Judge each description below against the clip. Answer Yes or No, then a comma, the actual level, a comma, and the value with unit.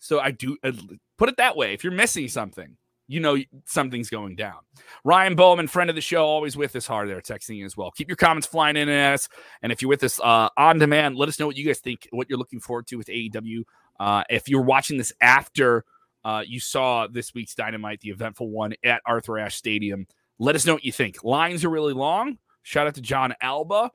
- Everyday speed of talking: No, fast, 235 wpm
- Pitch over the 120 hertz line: Yes, low, 130 Hz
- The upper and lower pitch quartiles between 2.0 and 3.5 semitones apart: No, average, 4.6 semitones